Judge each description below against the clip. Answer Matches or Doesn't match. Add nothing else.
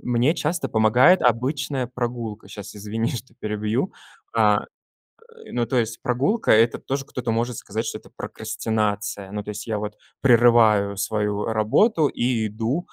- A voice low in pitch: Matches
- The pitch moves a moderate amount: Matches